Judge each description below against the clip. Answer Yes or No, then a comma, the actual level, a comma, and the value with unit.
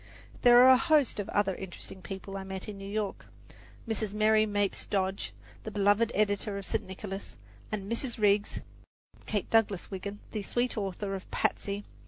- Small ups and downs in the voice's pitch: Yes, narrow, 1.8 semitones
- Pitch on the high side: Yes, high, 205 Hz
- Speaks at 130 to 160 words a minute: No, average, 170 wpm